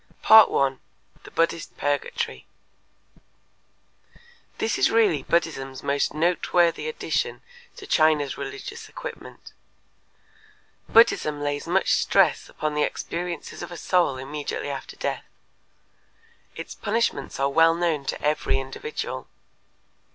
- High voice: No, medium, 160 Hz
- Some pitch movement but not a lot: Yes, average, 4.0 semitones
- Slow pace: Yes, slow, 105 wpm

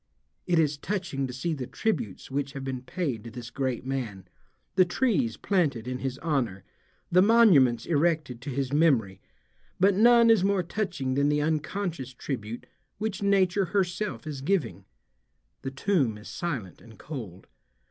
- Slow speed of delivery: No, average, 155 wpm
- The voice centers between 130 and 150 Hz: Yes, medium, 140 Hz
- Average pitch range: No, wide, 6.4 semitones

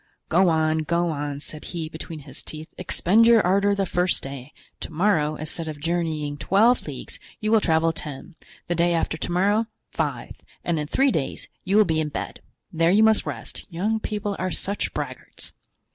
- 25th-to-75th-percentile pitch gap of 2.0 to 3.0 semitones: No, average, 4.4 semitones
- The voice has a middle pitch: Yes, medium, 170 Hz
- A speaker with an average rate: Yes, average, 190 wpm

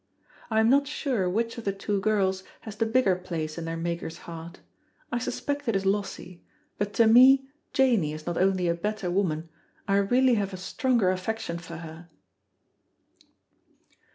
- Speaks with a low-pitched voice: No, high, 195 Hz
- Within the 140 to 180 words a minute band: Yes, average, 170 wpm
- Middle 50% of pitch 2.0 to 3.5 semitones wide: No, average, 4.9 semitones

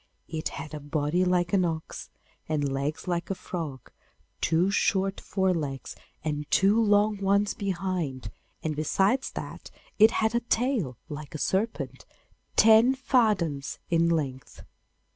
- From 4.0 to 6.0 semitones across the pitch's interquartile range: Yes, average, 5.1 semitones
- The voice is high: No, medium, 175 Hz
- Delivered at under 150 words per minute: Yes, average, 140 wpm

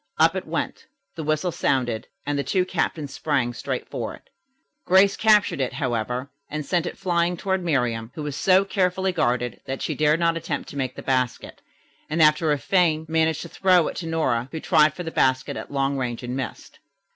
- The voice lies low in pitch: No, medium, 155 Hz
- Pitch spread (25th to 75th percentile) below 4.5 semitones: No, average, 4.8 semitones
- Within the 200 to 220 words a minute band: Yes, fast, 205 wpm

